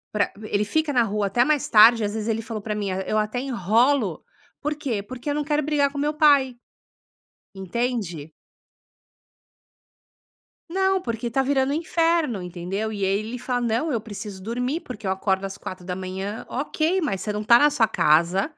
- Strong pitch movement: Yes, wide, 6.0 semitones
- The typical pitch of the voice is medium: No, high, 225 Hz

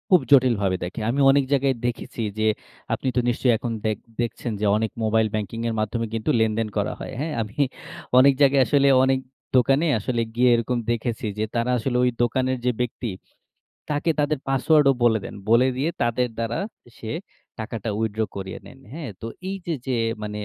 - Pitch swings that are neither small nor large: Yes, average, 3.2 semitones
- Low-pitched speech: Yes, low, 120 Hz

